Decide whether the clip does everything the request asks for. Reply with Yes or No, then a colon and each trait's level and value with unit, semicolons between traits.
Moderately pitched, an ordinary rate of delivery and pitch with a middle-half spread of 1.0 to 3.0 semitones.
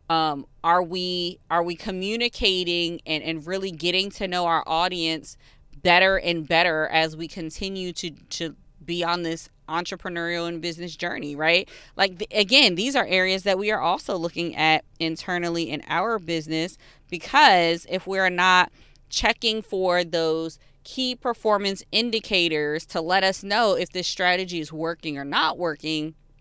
Yes: medium, 175 Hz; average, 155 wpm; average, 2.7 semitones